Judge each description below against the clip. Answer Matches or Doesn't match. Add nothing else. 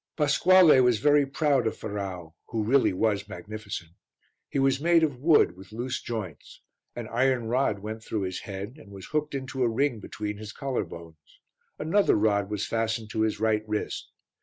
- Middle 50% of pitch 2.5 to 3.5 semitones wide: Doesn't match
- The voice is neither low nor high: Doesn't match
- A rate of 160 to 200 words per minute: Matches